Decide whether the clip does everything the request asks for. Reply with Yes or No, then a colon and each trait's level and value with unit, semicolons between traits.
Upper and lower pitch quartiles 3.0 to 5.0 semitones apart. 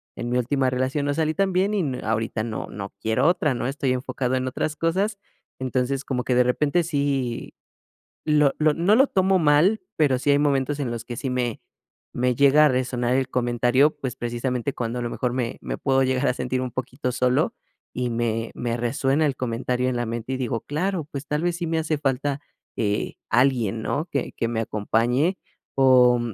Yes: average, 3.3 semitones